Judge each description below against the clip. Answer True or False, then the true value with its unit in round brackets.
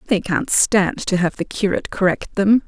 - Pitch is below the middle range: False (195 Hz)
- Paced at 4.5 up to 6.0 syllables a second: True (4.9 syllables/s)